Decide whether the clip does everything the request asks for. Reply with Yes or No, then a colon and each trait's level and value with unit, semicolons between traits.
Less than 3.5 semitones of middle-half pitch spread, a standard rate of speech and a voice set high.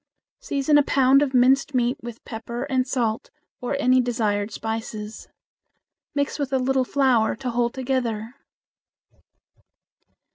No: average, 2.7 semitones; slow, 130 wpm; very high, 250 Hz